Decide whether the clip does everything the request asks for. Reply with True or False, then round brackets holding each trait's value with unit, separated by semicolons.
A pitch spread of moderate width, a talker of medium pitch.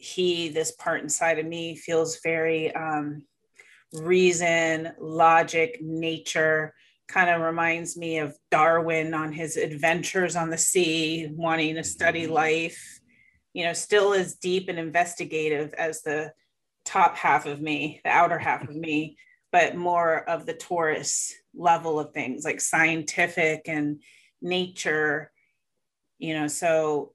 False (1.4 semitones; 165 Hz)